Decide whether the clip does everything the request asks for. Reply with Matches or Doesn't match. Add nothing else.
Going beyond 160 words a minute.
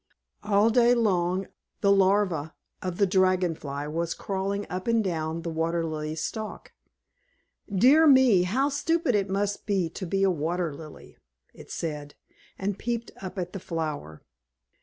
Doesn't match